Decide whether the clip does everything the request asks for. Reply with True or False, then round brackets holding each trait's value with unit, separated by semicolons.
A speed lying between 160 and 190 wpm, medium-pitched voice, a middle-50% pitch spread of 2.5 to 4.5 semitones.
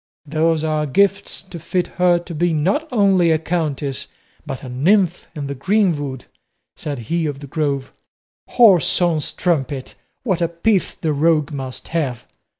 False (150 wpm; 160 Hz; 3.9 semitones)